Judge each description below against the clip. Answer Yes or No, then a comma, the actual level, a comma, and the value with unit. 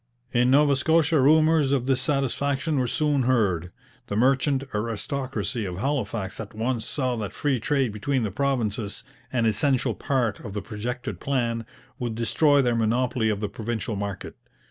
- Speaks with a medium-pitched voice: No, low, 125 Hz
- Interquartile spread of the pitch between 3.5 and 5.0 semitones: Yes, average, 4.1 semitones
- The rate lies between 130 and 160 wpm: Yes, average, 155 wpm